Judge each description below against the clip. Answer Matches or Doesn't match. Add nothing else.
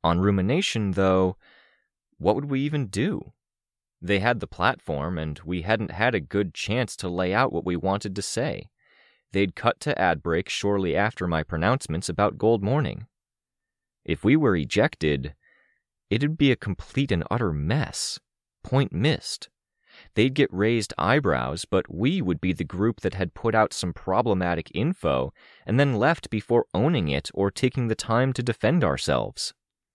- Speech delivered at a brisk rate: Doesn't match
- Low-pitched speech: Matches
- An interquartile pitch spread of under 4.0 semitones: Doesn't match